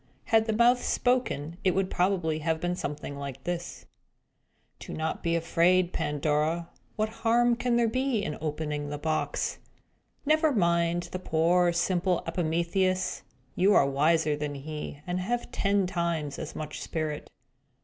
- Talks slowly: No, average, 150 wpm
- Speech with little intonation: No, average, 3.9 semitones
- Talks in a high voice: No, medium, 170 Hz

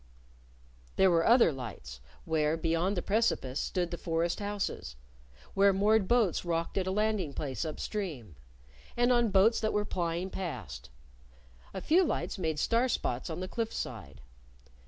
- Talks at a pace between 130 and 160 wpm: Yes, average, 155 wpm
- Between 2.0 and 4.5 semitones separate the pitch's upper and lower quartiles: No, average, 5.3 semitones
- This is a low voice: No, medium, 180 Hz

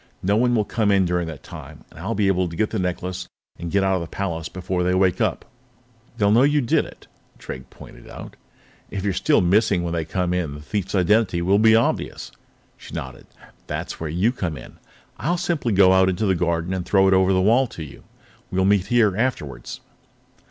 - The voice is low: Yes, very low, 95 Hz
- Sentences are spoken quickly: Yes, fast, 215 wpm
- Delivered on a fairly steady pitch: No, average, 3.3 semitones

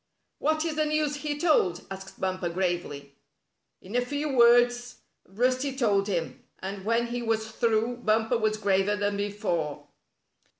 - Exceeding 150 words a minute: No, average, 145 wpm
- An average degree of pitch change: Yes, average, 4.3 semitones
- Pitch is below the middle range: No, high, 220 Hz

